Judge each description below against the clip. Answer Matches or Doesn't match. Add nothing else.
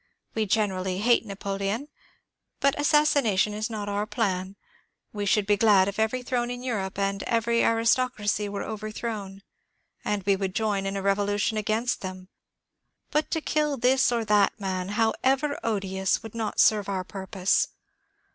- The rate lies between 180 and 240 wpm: Doesn't match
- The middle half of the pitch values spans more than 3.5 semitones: Doesn't match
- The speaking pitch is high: Matches